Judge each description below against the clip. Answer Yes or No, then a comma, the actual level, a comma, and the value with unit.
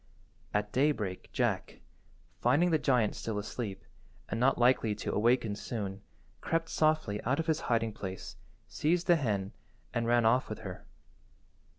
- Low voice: Yes, low, 115 Hz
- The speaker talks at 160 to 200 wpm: No, average, 145 wpm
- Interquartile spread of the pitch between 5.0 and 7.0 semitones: Yes, wide, 5.6 semitones